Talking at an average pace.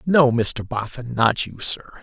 Yes: average, 180 wpm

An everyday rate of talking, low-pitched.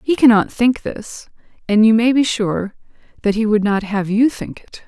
No: average, 195 wpm; high, 220 Hz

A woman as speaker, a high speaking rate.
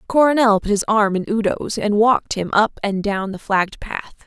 Yes: female; fast, 210 wpm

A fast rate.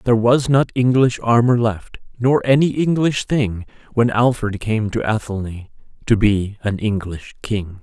No: average, 155 wpm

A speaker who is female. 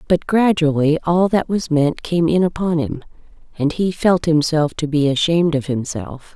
Yes: female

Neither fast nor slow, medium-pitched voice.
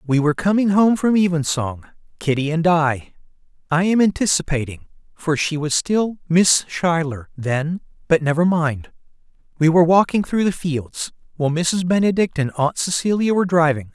Yes: average, 155 wpm; medium, 165 Hz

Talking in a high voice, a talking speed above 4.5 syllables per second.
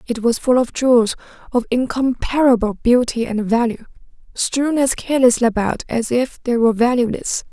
Yes: high, 240 Hz; 5.2 syllables/s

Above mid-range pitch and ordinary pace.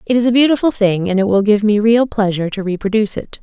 No: high, 215 Hz; fast, 265 wpm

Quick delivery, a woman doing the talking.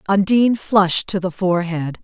No: average, 145 wpm; female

